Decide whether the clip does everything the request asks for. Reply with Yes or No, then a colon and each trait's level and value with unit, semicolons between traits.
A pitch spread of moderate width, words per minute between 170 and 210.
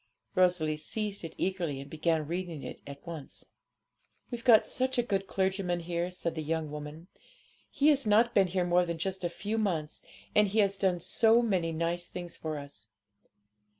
Yes: average, 3.6 semitones; average, 180 wpm